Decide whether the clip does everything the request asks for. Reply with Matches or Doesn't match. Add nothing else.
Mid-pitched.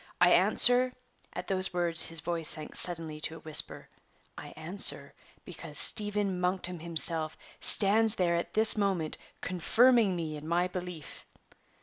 Matches